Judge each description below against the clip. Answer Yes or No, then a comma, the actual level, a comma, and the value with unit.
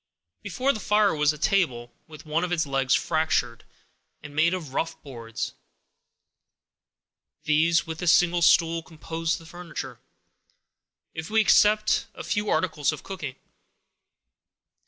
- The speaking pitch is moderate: Yes, medium, 165 Hz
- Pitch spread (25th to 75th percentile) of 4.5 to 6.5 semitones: No, average, 2.9 semitones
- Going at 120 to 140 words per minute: Yes, slow, 135 wpm